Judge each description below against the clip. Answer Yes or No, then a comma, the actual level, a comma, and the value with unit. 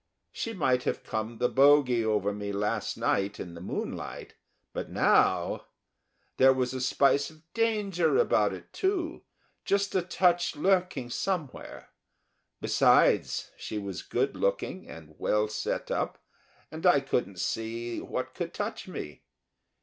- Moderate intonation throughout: No, wide, 9.0 semitones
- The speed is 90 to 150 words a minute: Yes, average, 140 wpm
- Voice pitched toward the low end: Yes, low, 130 Hz